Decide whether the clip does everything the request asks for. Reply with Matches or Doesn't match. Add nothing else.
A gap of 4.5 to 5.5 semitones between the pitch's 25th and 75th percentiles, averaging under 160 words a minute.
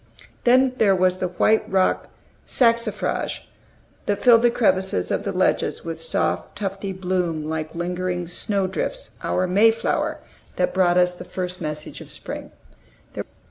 Doesn't match